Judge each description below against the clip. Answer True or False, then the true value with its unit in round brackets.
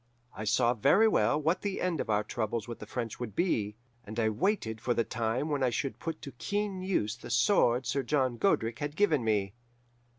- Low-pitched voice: True (125 Hz)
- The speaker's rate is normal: False (210 wpm)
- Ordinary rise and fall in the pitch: False (6.3 semitones)